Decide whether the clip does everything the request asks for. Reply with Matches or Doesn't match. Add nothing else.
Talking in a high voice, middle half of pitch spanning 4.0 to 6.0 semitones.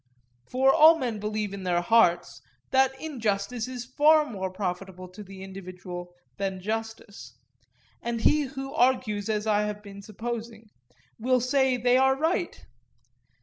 Matches